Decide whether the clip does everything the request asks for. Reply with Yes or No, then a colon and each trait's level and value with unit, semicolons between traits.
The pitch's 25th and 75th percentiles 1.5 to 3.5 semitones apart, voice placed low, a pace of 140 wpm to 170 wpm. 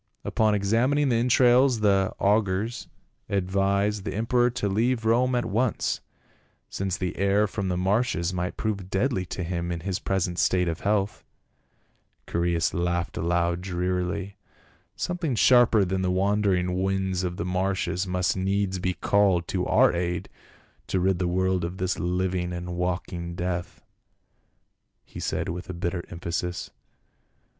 Yes: narrow, 2.6 semitones; very low, 95 Hz; average, 150 wpm